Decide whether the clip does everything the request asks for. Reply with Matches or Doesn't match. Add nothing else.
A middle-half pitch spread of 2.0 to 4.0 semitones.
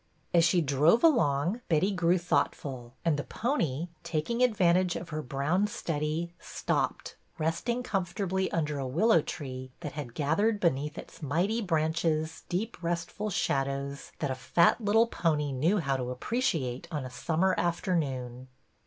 Doesn't match